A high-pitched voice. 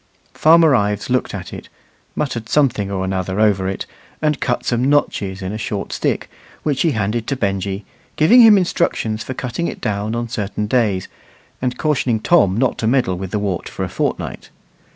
No: low, 110 Hz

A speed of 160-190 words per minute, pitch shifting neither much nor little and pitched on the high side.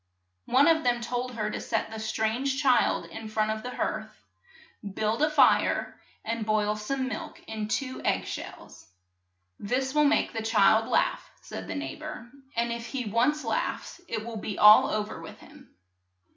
Yes: average, 185 wpm; average, 3.4 semitones; high, 235 Hz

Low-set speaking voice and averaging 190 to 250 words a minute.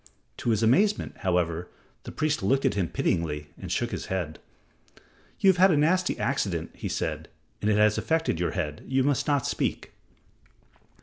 No: low, 110 Hz; average, 175 wpm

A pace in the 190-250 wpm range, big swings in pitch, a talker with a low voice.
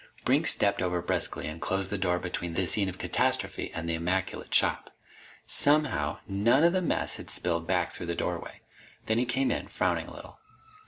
Yes: average, 195 wpm; wide, 5.9 semitones; very low, 95 Hz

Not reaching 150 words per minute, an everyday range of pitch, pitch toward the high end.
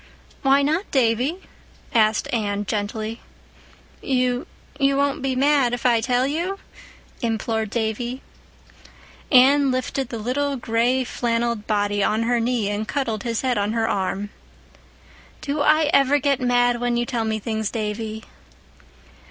Yes: slow, 135 wpm; average, 3.6 semitones; high, 240 Hz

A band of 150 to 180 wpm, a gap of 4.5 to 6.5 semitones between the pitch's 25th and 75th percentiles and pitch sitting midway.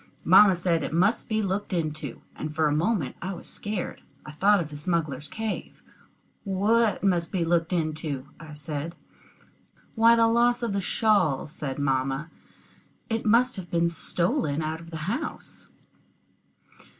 Yes: average, 155 wpm; average, 5.2 semitones; medium, 170 Hz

